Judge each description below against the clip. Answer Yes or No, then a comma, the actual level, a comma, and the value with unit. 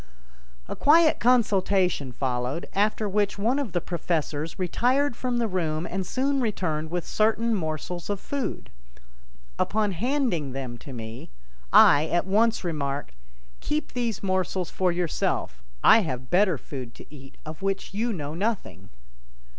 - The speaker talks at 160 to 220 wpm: No, average, 145 wpm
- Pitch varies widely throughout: Yes, wide, 6.4 semitones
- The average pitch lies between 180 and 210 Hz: Yes, medium, 185 Hz